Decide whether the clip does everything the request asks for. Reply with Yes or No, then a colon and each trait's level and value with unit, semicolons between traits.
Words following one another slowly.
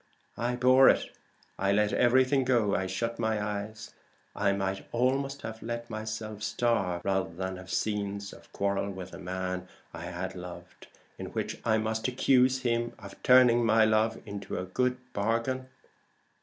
No: average, 160 wpm